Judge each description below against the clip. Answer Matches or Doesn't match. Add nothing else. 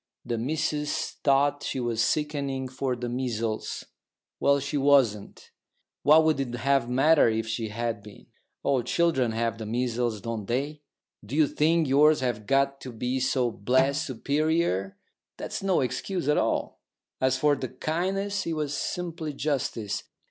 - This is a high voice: Doesn't match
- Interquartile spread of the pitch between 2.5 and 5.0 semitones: Matches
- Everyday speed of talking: Matches